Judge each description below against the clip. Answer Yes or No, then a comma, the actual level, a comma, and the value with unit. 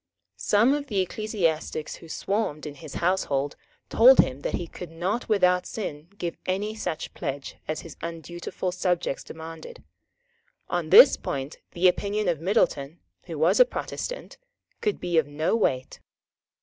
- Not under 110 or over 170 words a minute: Yes, average, 150 wpm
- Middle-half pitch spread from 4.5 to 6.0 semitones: Yes, average, 4.9 semitones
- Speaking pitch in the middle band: Yes, medium, 175 Hz